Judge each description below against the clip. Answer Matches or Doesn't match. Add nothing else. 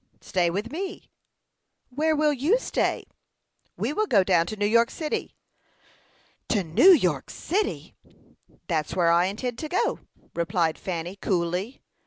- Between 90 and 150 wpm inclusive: Matches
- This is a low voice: Doesn't match